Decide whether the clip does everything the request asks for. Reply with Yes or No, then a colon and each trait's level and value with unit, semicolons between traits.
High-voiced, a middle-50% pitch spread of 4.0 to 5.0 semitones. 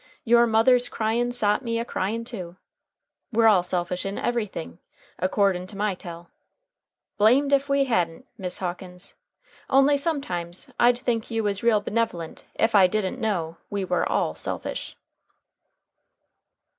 Yes: high, 215 Hz; average, 4.6 semitones